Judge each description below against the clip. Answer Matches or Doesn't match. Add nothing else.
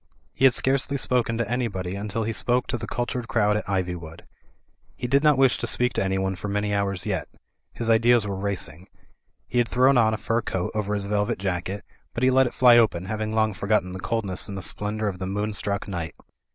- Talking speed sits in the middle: Doesn't match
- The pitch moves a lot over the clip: Doesn't match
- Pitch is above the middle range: Doesn't match